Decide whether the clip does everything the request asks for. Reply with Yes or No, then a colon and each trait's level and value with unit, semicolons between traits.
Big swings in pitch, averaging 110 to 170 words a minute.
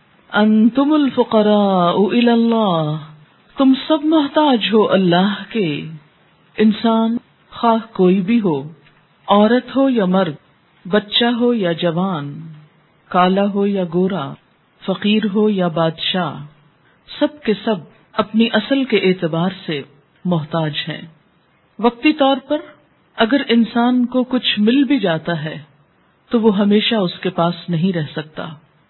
Yes: wide, 5.8 semitones; average, 125 wpm